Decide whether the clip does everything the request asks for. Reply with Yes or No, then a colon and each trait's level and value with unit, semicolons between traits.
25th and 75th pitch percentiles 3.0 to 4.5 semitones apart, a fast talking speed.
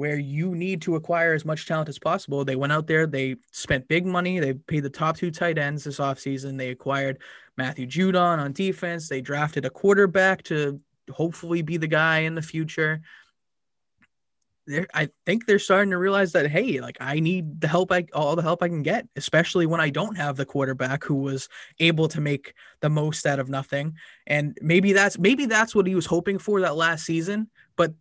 Yes: average, 3.7 semitones; fast, 210 wpm